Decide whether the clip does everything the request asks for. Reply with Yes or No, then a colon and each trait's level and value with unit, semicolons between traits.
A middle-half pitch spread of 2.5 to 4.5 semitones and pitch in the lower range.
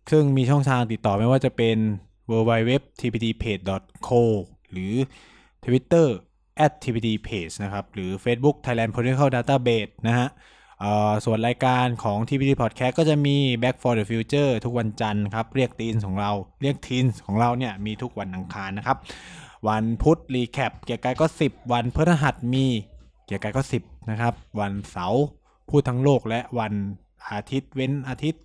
Yes: average, 3.8 semitones; low, 120 Hz